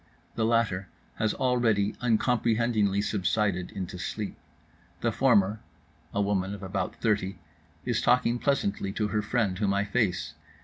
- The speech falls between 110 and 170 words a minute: Yes, slow, 135 wpm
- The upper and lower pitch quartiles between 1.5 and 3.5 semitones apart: Yes, average, 2.8 semitones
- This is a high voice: No, low, 105 Hz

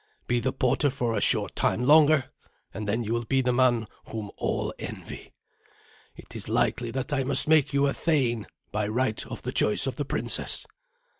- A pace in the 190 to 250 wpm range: Yes, average, 195 wpm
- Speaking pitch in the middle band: No, low, 125 Hz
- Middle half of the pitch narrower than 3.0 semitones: No, average, 3.3 semitones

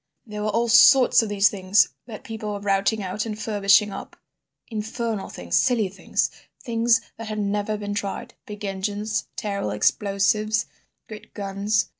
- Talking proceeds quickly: No, average, 155 wpm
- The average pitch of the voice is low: No, high, 210 Hz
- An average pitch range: No, narrow, 1.7 semitones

